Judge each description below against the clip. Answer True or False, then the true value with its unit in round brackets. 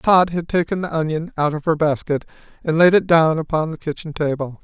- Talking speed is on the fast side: True (220 wpm)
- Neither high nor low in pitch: True (160 Hz)